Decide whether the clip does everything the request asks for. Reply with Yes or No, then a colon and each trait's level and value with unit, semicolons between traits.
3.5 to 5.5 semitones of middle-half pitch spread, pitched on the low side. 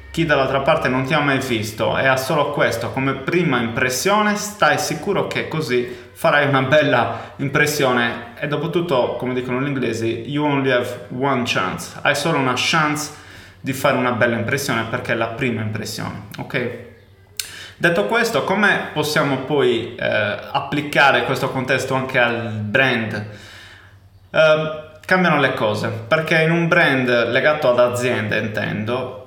Yes: average, 4.0 semitones; low, 130 Hz